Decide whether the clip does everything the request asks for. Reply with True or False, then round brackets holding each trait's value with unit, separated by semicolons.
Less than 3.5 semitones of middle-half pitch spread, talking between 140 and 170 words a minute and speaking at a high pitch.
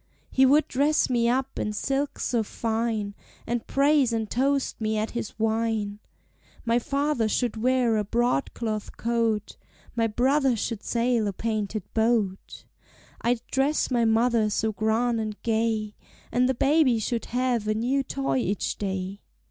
True (2.8 semitones; 155 wpm; 230 Hz)